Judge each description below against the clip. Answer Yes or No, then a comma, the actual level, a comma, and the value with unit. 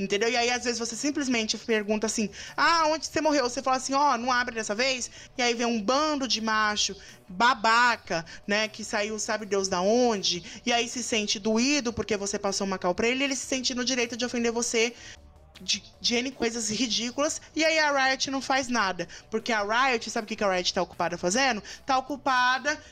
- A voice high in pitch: Yes, high, 235 Hz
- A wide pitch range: No, average, 3.4 semitones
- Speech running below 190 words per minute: No, fast, 215 wpm